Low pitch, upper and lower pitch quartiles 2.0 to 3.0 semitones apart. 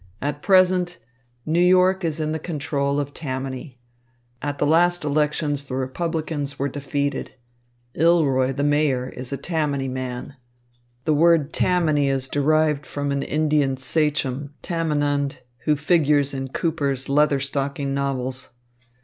No: medium, 145 Hz; narrow, 2.4 semitones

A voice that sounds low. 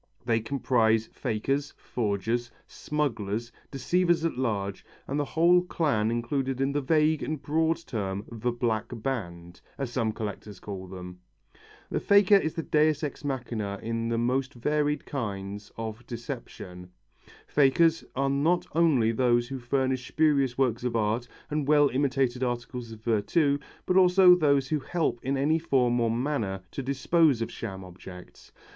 Yes: low, 125 Hz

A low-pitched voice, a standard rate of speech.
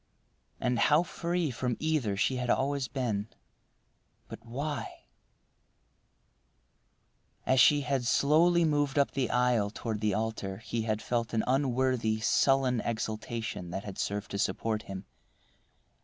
No: low, 125 Hz; slow, 125 wpm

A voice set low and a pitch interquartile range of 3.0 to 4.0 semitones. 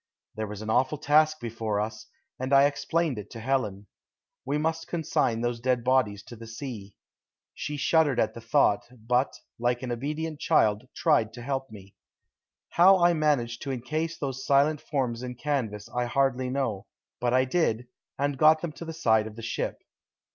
No: low, 130 Hz; average, 4.4 semitones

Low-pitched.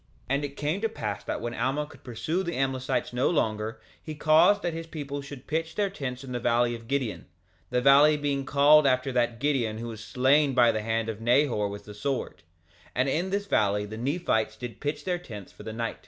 Yes: low, 130 Hz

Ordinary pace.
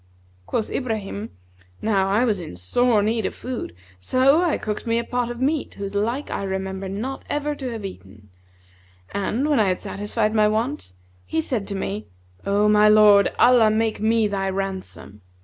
Yes: average, 180 wpm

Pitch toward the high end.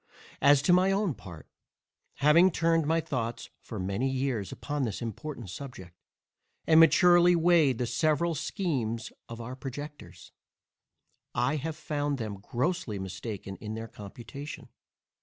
No: low, 135 Hz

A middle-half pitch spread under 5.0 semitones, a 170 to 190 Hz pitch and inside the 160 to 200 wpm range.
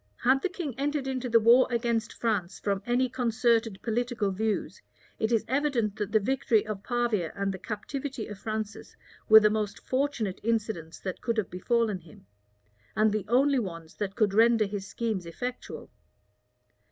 No: average, 3.1 semitones; high, 220 Hz; average, 165 wpm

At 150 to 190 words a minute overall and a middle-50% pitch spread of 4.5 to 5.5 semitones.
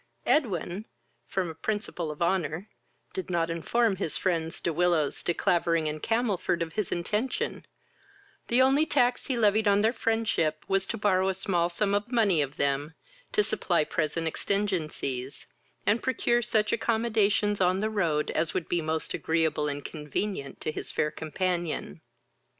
Yes: average, 160 wpm; average, 4.8 semitones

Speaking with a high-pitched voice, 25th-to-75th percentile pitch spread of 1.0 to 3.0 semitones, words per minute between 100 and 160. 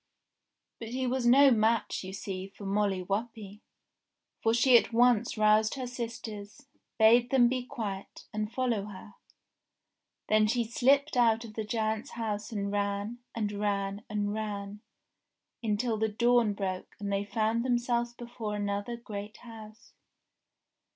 Yes: high, 220 Hz; average, 2.7 semitones; average, 145 wpm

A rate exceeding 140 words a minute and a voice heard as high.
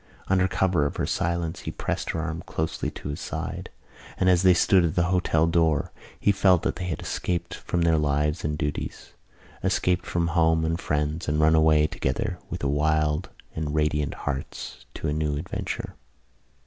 No: average, 180 wpm; very low, 80 Hz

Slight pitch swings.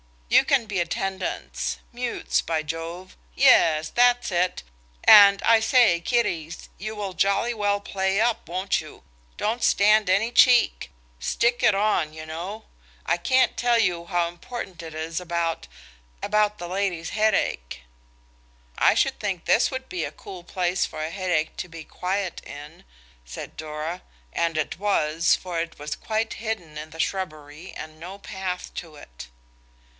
No: average, 4.5 semitones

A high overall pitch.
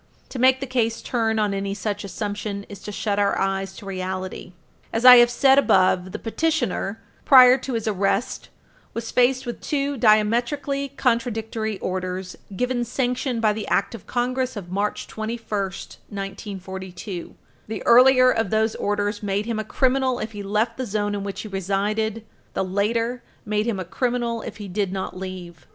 Yes: high, 215 Hz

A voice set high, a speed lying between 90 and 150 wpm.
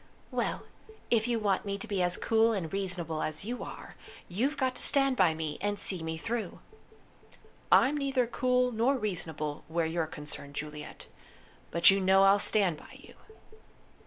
No: high, 195 Hz; average, 170 wpm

